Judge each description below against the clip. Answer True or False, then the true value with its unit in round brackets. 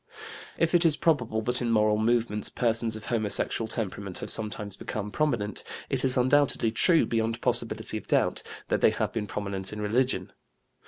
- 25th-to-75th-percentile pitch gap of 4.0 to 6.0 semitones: False (3.0 semitones)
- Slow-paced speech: False (170 wpm)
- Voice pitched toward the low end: True (115 Hz)